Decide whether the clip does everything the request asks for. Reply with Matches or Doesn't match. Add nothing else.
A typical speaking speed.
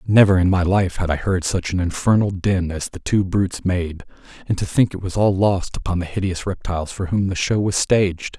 Doesn't match